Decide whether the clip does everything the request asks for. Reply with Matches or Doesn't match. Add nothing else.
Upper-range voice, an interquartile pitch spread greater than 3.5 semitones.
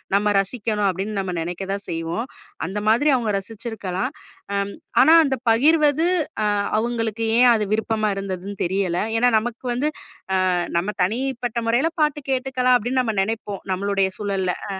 Matches